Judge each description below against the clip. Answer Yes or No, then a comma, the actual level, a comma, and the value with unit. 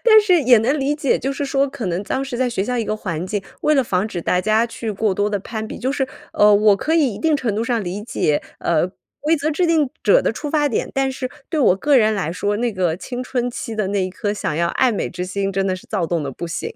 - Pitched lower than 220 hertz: No, high, 225 Hz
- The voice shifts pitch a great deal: Yes, wide, 5.7 semitones